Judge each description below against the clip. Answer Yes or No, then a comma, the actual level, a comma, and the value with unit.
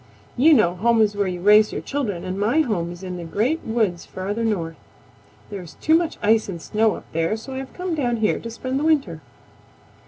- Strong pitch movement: Yes, wide, 6.0 semitones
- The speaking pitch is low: No, high, 215 Hz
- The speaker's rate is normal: No, fast, 225 wpm